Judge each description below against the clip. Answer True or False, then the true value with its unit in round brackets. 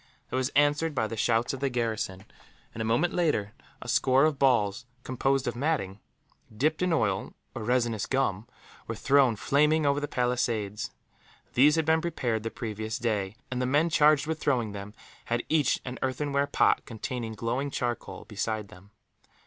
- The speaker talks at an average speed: True (175 wpm)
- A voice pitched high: False (125 Hz)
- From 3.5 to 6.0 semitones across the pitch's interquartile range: True (4.4 semitones)